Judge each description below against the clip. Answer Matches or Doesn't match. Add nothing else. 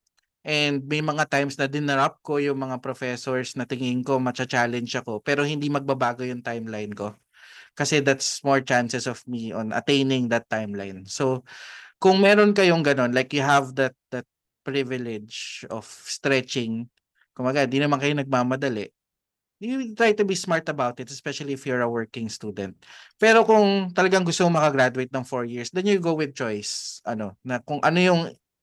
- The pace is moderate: Doesn't match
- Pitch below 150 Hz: Matches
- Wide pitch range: Doesn't match